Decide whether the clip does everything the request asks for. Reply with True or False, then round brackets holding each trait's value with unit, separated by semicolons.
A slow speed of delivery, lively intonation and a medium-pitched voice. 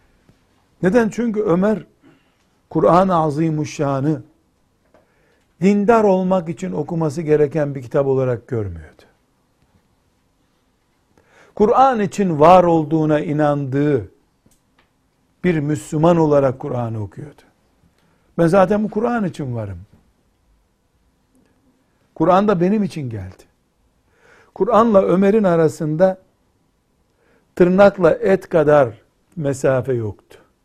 True (85 wpm; 6.2 semitones; 155 Hz)